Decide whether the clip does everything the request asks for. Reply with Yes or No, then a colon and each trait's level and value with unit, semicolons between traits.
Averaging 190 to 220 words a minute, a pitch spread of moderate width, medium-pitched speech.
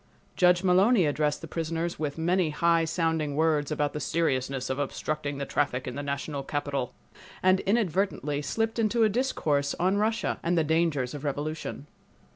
No: average, 165 wpm; average, 3.8 semitones; medium, 155 Hz